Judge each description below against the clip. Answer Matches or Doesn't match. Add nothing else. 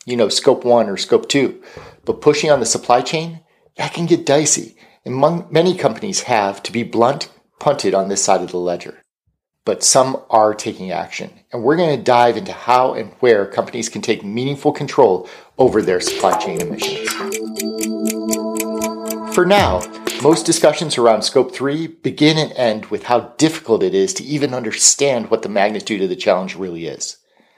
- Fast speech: Doesn't match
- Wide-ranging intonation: Matches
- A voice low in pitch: Matches